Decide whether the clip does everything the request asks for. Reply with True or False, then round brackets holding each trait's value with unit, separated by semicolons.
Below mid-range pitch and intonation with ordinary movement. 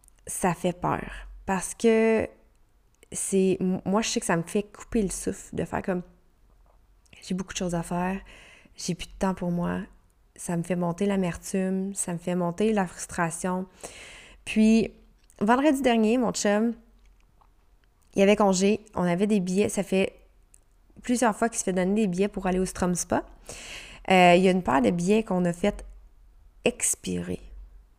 False (190 Hz; 3.0 semitones)